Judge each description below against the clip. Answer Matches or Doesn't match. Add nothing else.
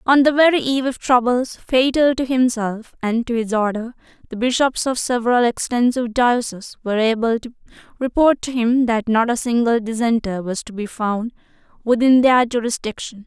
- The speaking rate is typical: Matches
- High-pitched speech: Matches